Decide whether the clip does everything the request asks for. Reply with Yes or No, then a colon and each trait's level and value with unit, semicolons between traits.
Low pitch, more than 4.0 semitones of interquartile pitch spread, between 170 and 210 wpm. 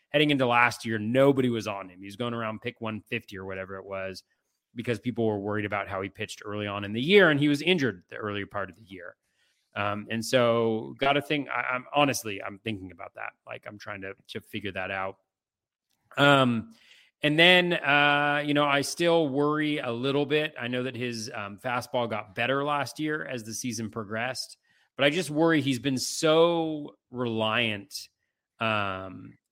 Yes: low, 120 Hz; wide, 5.4 semitones; average, 200 wpm